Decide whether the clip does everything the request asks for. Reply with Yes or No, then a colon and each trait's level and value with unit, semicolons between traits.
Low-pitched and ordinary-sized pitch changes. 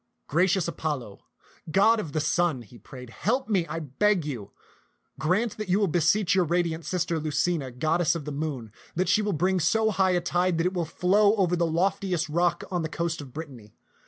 No: medium, 170 Hz; average, 3.5 semitones